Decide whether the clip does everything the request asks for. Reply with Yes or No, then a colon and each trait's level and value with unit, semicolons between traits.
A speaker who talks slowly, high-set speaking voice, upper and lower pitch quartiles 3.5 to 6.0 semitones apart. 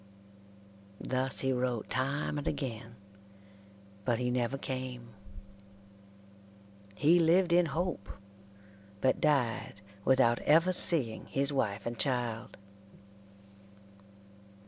No: slow, 95 wpm; low, 130 Hz; average, 3.9 semitones